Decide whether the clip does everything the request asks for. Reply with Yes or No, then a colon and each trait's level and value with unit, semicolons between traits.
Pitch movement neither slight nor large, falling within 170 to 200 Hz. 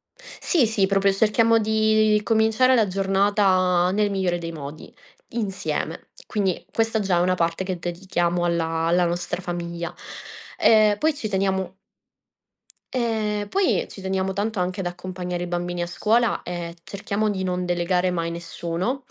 Yes: average, 3.3 semitones; high, 190 Hz